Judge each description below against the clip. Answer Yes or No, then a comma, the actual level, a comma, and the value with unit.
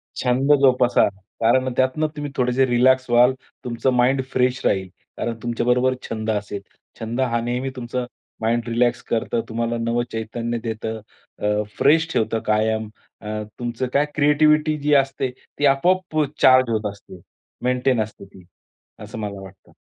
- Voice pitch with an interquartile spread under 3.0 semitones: Yes, narrow, 2.6 semitones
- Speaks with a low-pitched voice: Yes, low, 120 Hz